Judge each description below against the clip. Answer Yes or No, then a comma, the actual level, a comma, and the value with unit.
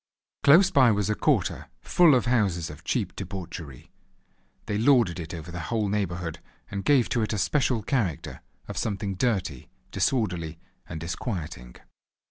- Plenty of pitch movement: Yes, wide, 5.8 semitones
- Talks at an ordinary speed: Yes, average, 150 wpm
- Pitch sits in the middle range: No, low, 100 Hz